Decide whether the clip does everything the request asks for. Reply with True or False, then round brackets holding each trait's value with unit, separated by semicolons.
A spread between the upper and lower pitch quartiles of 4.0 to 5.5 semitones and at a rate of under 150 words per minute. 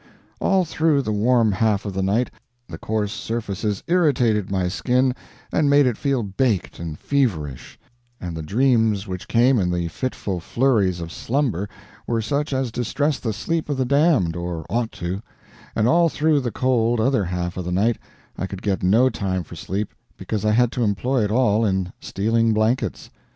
False (5.2 semitones; 180 wpm)